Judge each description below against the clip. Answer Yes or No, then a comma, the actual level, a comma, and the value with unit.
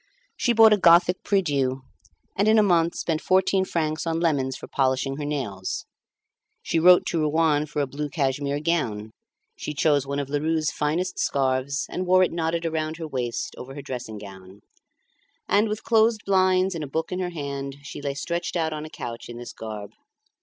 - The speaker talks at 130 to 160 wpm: No, average, 195 wpm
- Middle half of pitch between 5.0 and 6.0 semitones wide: No, average, 4.3 semitones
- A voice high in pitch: No, medium, 155 Hz